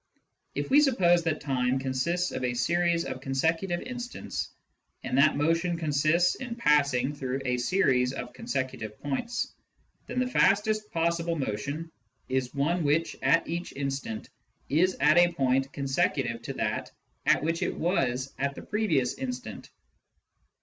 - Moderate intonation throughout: Yes, average, 4.7 semitones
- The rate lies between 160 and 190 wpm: No, average, 150 wpm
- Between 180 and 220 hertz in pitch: No, medium, 150 Hz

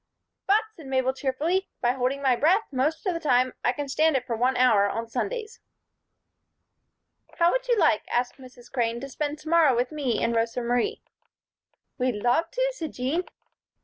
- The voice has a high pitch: Yes, very high, 265 Hz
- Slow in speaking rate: No, average, 180 wpm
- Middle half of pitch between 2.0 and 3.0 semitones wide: No, average, 5.1 semitones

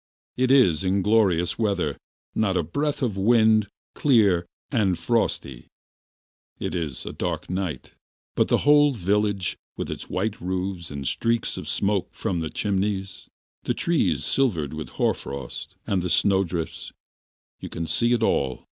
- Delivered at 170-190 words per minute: No, average, 145 wpm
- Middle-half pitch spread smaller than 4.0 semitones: No, average, 4.5 semitones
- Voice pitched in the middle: No, very low, 95 Hz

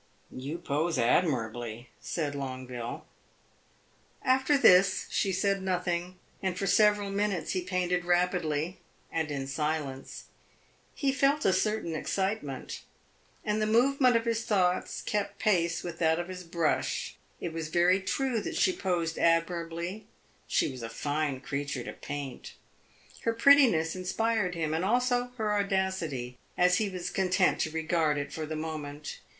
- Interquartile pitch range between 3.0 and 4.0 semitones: No, average, 4.6 semitones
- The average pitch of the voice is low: No, medium, 175 Hz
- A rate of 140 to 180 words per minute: Yes, average, 145 wpm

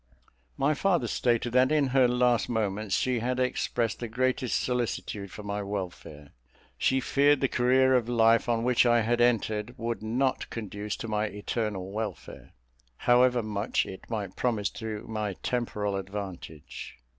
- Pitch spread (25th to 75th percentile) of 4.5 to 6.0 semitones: No, average, 3.3 semitones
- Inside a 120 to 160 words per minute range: Yes, average, 155 wpm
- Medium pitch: No, low, 115 Hz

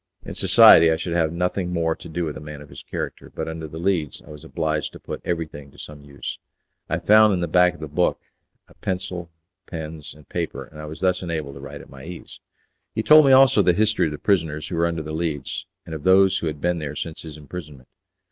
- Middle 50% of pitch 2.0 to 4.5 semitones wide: Yes, average, 2.8 semitones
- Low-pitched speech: Yes, very low, 80 Hz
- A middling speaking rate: No, fast, 250 wpm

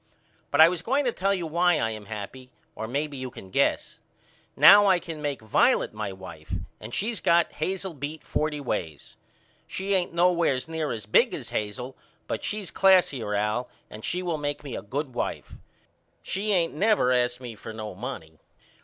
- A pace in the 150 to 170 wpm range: No, average, 185 wpm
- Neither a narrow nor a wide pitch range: No, wide, 8.1 semitones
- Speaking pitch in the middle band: Yes, medium, 145 Hz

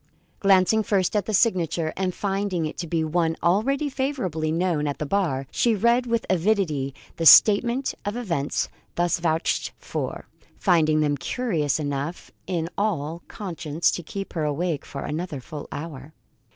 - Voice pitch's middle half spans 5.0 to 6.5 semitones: No, average, 4.6 semitones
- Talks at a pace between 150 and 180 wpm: Yes, average, 155 wpm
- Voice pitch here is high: No, medium, 175 Hz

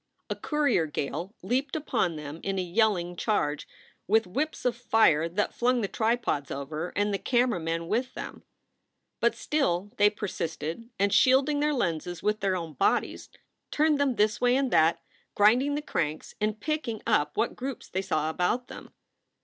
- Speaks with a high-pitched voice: Yes, high, 210 Hz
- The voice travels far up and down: Yes, wide, 6.6 semitones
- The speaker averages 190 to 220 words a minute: No, average, 170 wpm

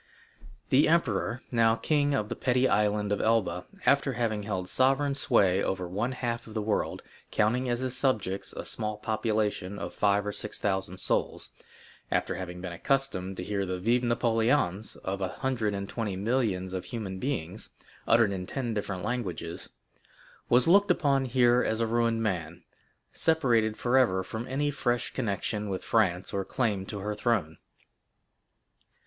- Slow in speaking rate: No, average, 155 wpm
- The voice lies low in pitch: Yes, low, 110 Hz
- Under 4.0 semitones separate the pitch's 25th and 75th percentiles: No, average, 4.3 semitones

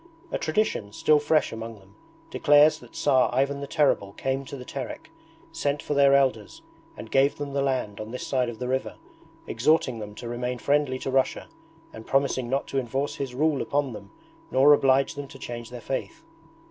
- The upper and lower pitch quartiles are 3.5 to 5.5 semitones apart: No, average, 2.9 semitones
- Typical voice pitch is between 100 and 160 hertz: Yes, low, 135 Hz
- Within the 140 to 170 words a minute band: No, average, 195 wpm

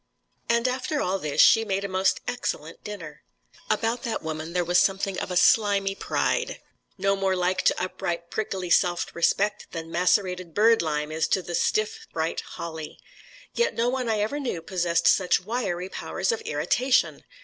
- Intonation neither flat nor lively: Yes, average, 4.5 semitones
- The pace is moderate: Yes, average, 170 wpm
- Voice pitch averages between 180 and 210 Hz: Yes, high, 190 Hz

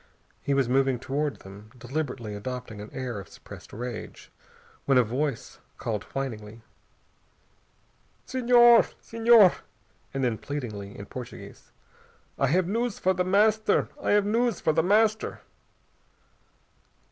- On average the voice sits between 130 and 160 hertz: Yes, low, 135 Hz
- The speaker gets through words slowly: Yes, slow, 125 wpm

